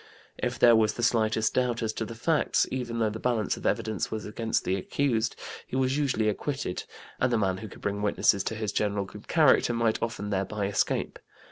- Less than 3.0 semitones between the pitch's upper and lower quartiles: Yes, narrow, 2.6 semitones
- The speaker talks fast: Yes, fast, 210 wpm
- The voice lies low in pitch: Yes, low, 110 Hz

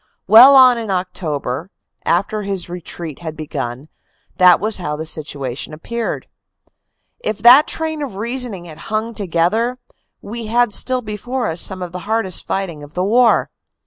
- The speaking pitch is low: No, high, 195 Hz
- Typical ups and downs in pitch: No, wide, 5.9 semitones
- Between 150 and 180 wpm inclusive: Yes, average, 160 wpm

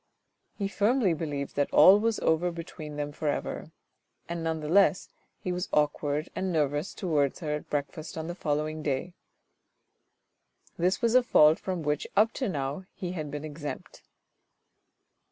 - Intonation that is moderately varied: Yes, average, 3.8 semitones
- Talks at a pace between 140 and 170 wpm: Yes, average, 160 wpm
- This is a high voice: No, medium, 160 Hz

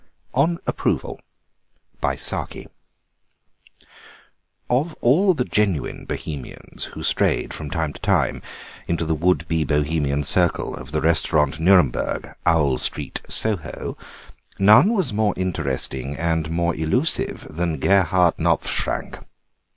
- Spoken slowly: Yes, slow, 110 wpm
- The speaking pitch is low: Yes, very low, 80 Hz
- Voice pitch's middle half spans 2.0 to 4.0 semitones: No, average, 4.7 semitones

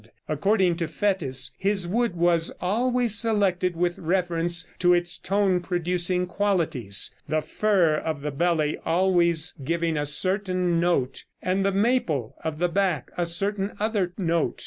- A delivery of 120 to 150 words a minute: Yes, average, 145 wpm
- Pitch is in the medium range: Yes, medium, 175 Hz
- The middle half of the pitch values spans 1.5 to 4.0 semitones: Yes, average, 2.9 semitones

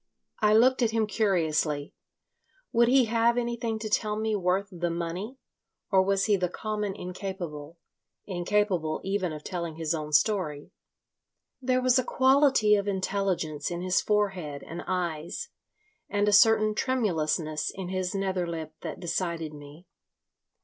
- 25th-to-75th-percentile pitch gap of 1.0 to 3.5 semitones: No, average, 4.3 semitones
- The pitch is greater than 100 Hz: Yes, high, 190 Hz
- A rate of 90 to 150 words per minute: Yes, average, 145 wpm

